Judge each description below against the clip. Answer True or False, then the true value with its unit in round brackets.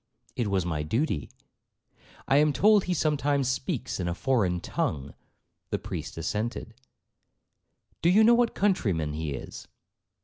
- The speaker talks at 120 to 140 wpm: True (135 wpm)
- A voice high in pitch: False (120 Hz)